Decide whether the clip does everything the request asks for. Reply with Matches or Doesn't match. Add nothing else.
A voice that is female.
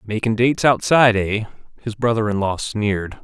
Doesn't match